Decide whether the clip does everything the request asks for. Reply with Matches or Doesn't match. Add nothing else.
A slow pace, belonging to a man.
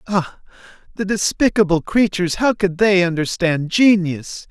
Matches